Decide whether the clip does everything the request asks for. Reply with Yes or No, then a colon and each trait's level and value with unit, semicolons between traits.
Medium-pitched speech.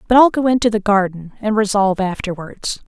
No: high, 205 Hz